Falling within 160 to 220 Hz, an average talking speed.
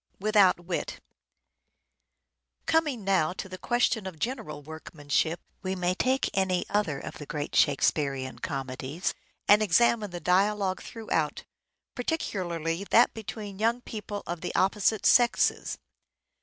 No: high, 190 Hz; slow, 130 wpm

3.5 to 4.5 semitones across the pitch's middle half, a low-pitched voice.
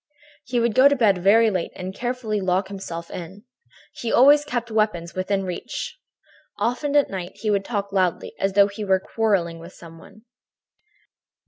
No: average, 3.9 semitones; high, 200 Hz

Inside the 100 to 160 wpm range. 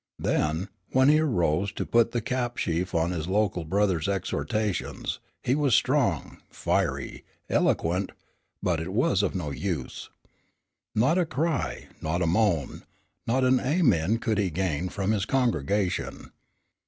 Yes: average, 140 wpm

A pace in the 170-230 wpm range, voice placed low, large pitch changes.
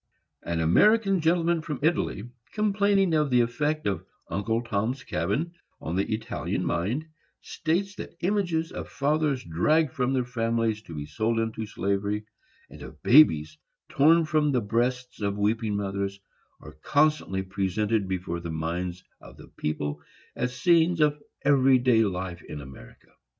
No: average, 150 wpm; low, 115 Hz; wide, 7.9 semitones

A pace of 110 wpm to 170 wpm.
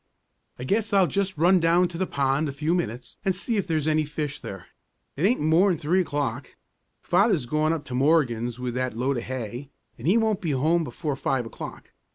No: fast, 205 wpm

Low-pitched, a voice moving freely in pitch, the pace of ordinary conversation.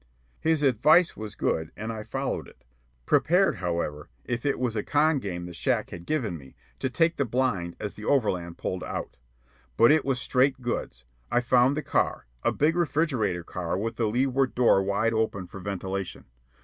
Yes: low, 115 Hz; wide, 6.4 semitones; average, 185 wpm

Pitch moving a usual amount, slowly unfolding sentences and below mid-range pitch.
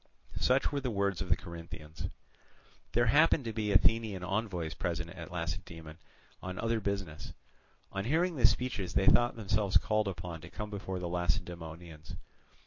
No: average, 4.5 semitones; average, 155 wpm; very low, 95 Hz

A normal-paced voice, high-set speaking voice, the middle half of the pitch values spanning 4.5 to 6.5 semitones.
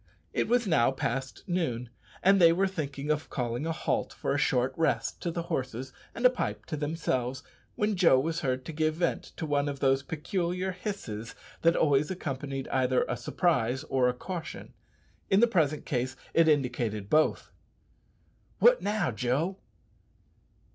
No: average, 165 wpm; medium, 150 Hz; average, 5.2 semitones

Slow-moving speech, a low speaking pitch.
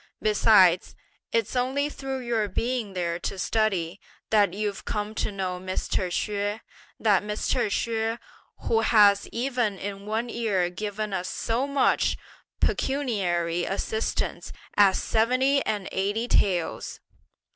No: slow, 125 wpm; high, 210 Hz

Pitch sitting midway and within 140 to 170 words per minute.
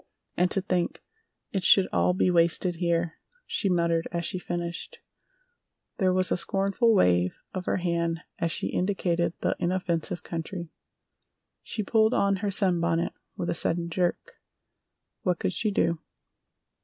Yes: medium, 175 Hz; average, 145 wpm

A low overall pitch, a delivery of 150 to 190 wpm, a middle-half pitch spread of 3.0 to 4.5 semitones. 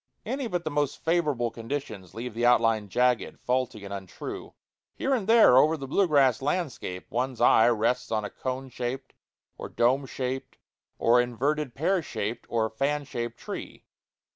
Yes: low, 125 Hz; average, 165 wpm; average, 4.2 semitones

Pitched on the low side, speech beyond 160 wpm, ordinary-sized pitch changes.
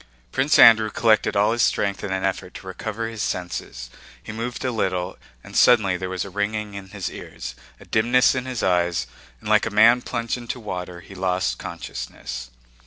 Yes: low, 105 Hz; average, 190 wpm; average, 3.7 semitones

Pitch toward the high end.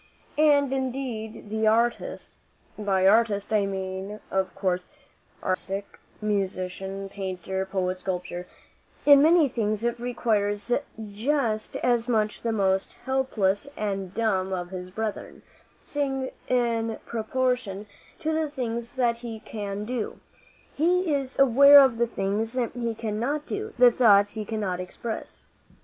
Yes: high, 220 Hz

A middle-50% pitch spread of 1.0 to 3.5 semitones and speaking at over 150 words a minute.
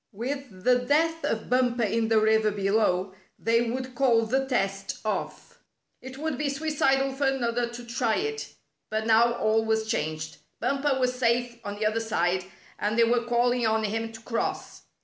Yes: average, 3.0 semitones; average, 175 wpm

